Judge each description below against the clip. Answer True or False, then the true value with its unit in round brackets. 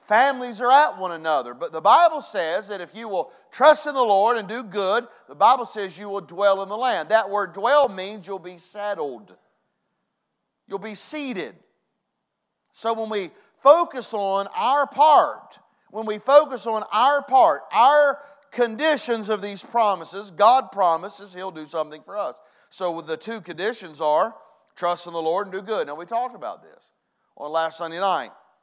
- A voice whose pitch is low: False (210 Hz)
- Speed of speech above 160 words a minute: True (180 wpm)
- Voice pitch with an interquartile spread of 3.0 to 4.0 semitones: False (5.1 semitones)